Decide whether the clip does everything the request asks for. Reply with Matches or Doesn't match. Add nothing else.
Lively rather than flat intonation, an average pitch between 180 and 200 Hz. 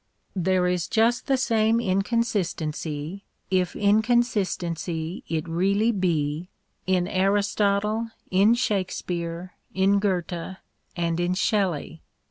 Doesn't match